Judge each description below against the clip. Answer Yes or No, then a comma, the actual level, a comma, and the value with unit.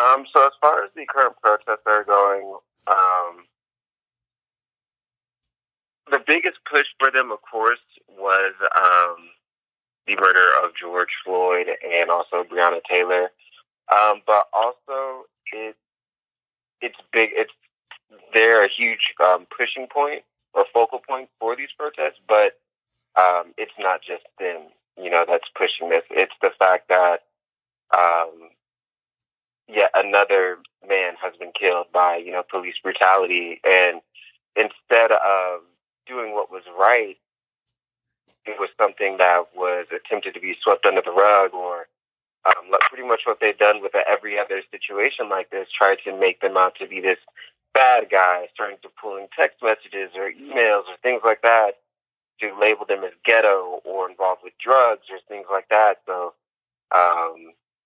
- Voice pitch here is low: Yes, low, 100 Hz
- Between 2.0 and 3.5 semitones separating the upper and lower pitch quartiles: No, average, 5.2 semitones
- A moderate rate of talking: Yes, average, 150 wpm